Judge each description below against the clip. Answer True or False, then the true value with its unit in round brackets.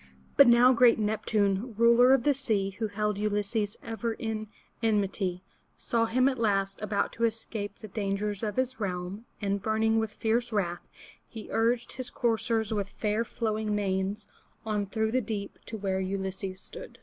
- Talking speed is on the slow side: False (165 wpm)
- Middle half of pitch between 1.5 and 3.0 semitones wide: True (2.4 semitones)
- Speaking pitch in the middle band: False (215 Hz)